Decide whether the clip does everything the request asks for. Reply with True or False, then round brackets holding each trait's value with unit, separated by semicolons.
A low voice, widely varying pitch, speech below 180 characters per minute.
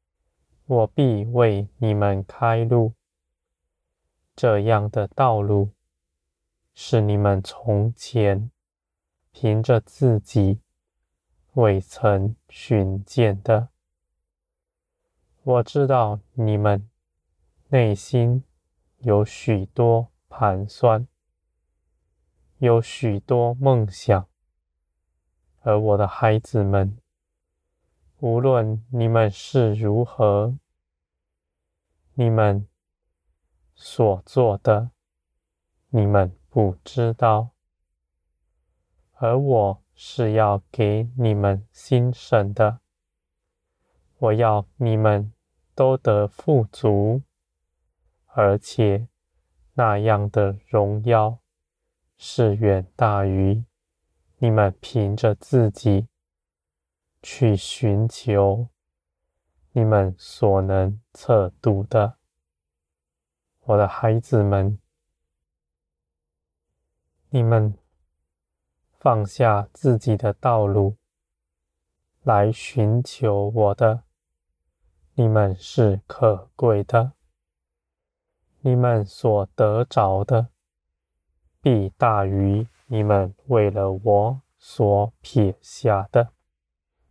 True (100 Hz; 6.8 semitones; 105 characters per minute)